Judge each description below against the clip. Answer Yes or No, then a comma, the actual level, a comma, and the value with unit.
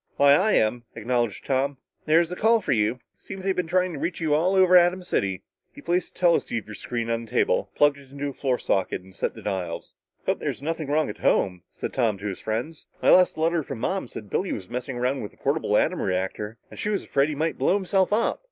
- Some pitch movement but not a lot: No, wide, 7.7 semitones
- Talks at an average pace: No, fast, 240 wpm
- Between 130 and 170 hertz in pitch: Yes, medium, 140 Hz